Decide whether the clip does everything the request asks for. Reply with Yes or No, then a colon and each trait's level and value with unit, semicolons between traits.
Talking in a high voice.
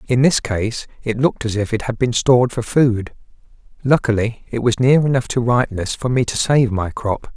No: low, 120 Hz